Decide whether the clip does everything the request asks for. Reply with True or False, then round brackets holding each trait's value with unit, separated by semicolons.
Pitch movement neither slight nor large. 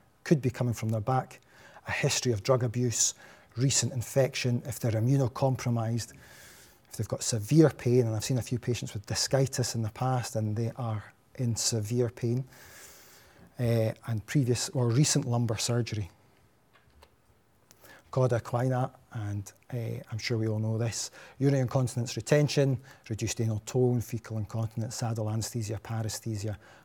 False (2.3 semitones)